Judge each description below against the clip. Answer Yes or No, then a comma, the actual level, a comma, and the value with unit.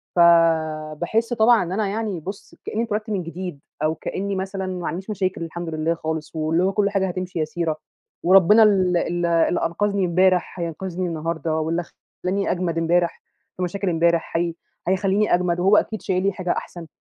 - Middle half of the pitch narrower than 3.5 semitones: Yes, narrow, 2.6 semitones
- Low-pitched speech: No, medium, 180 Hz